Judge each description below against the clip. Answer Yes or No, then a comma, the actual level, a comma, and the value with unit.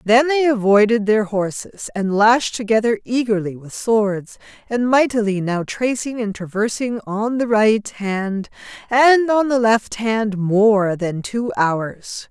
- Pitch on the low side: No, high, 220 Hz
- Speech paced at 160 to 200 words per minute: No, average, 145 wpm